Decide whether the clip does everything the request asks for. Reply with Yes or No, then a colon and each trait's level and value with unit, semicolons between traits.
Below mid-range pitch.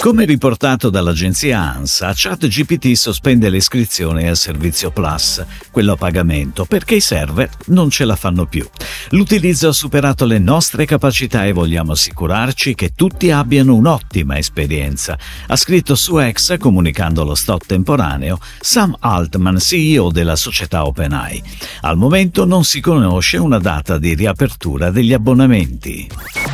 Yes: low, 105 Hz